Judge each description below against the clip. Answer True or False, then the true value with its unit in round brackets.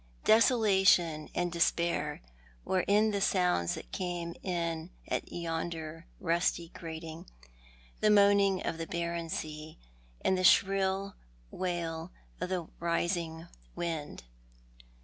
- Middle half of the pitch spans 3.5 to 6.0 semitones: False (2.6 semitones)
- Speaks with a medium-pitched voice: True (170 Hz)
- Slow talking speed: True (110 wpm)